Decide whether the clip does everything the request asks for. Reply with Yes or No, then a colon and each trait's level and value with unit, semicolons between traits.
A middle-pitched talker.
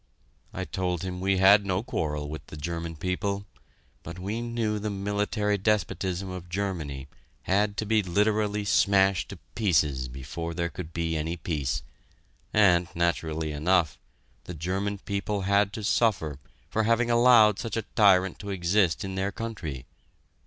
No: very low, 95 Hz